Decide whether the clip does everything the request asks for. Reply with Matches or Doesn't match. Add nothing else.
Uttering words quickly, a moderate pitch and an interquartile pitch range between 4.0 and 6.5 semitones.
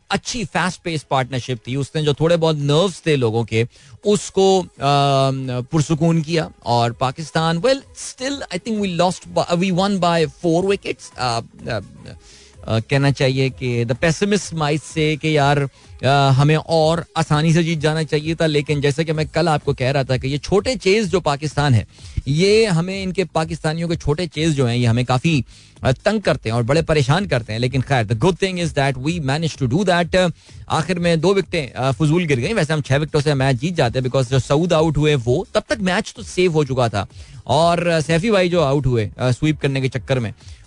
Matches